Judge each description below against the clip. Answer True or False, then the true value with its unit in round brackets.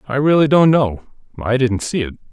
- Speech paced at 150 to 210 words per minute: True (205 wpm)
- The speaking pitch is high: False (130 Hz)